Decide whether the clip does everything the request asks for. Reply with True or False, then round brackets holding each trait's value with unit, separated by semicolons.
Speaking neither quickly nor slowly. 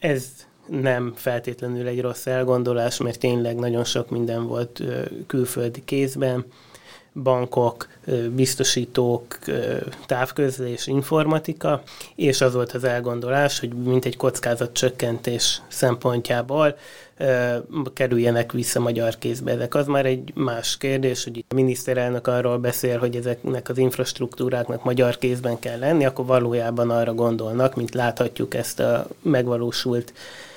True (120 wpm)